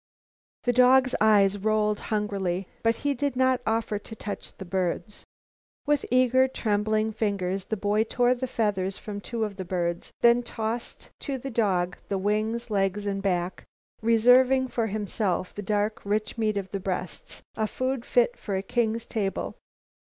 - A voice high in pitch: Yes, high, 215 Hz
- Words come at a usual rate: Yes, average, 165 wpm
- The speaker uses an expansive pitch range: No, average, 3.3 semitones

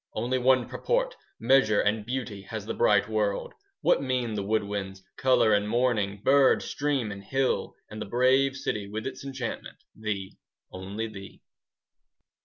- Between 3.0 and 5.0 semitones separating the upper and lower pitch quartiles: Yes, average, 4.1 semitones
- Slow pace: No, average, 165 wpm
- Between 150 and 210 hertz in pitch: No, low, 110 Hz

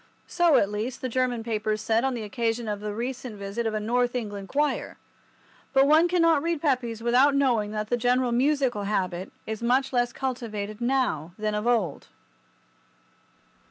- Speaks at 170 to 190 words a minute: Yes, average, 175 wpm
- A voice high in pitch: Yes, high, 235 Hz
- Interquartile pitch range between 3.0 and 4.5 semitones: Yes, average, 3.5 semitones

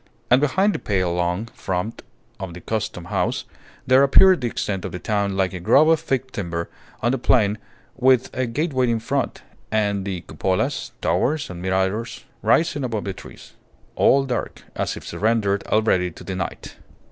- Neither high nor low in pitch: No, low, 110 Hz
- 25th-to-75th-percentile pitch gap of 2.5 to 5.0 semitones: No, wide, 5.6 semitones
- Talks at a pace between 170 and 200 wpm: Yes, average, 175 wpm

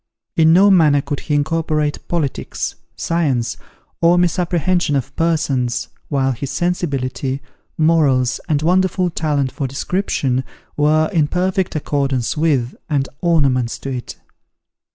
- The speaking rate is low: Yes, slow, 120 wpm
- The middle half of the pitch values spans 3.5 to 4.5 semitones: Yes, average, 3.9 semitones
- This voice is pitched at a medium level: Yes, medium, 150 Hz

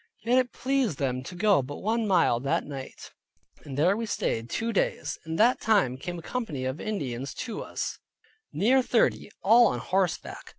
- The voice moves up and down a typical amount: No, wide, 8.7 semitones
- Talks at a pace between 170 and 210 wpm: Yes, average, 180 wpm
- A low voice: No, high, 190 Hz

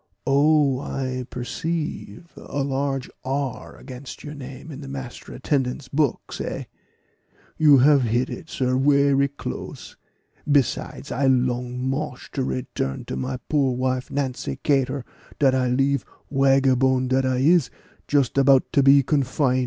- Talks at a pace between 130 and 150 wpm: Yes, average, 140 wpm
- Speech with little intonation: Yes, narrow, 1.7 semitones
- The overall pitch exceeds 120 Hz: Yes, low, 135 Hz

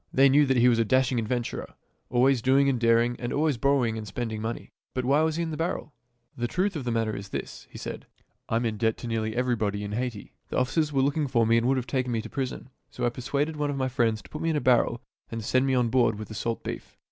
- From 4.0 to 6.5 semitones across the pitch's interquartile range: No, average, 3.0 semitones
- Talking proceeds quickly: Yes, fast, 280 wpm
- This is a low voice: Yes, low, 125 Hz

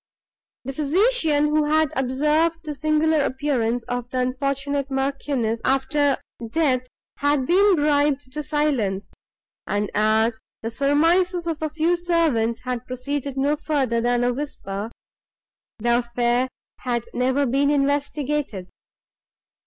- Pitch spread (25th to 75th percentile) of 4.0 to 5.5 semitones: No, average, 3.5 semitones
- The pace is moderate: No, slow, 130 wpm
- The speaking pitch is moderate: No, very high, 275 Hz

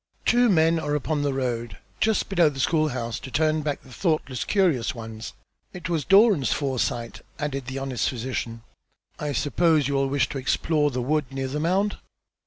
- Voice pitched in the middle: Yes, medium, 145 Hz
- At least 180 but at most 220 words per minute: Yes, average, 185 wpm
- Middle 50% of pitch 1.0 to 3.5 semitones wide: No, average, 3.9 semitones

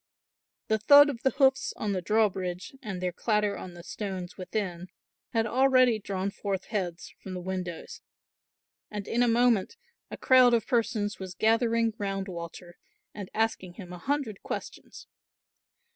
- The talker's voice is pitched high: Yes, high, 205 Hz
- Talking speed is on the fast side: No, average, 155 wpm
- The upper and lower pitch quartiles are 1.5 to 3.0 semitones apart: No, average, 4.0 semitones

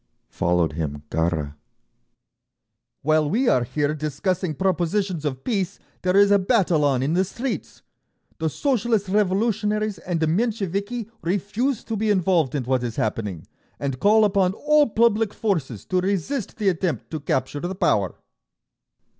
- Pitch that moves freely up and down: Yes, wide, 6.5 semitones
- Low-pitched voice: No, medium, 185 Hz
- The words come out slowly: No, average, 145 wpm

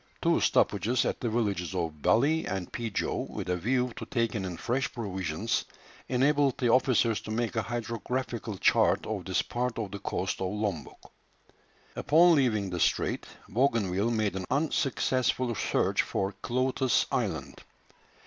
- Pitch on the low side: Yes, low, 115 Hz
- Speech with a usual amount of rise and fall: Yes, average, 4.5 semitones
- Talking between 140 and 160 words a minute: Yes, average, 150 wpm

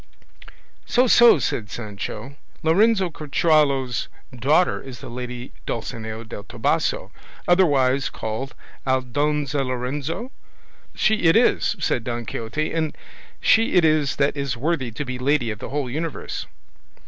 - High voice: No, medium, 140 Hz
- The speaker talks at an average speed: No, slow, 130 wpm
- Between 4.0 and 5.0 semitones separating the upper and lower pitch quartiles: Yes, average, 4.6 semitones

